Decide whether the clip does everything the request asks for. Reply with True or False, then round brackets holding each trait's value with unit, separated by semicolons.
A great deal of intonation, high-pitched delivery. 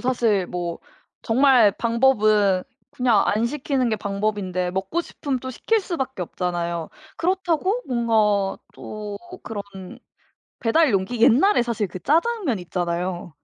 True (5.7 semitones; 220 Hz)